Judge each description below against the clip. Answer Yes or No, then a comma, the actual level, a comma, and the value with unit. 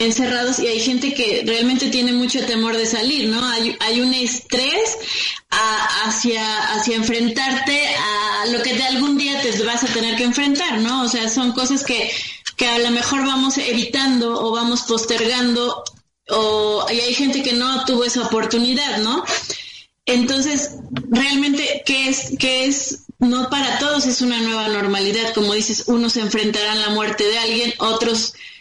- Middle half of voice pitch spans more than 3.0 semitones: No, narrow, 2.5 semitones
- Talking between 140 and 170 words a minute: Yes, average, 165 wpm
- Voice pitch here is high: Yes, high, 240 Hz